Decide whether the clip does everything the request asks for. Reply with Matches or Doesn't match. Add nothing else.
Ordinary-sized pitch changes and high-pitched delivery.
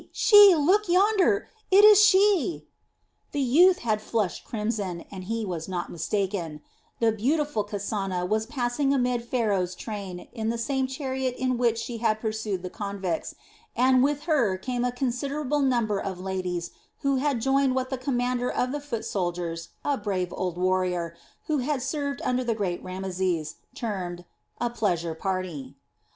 Doesn't match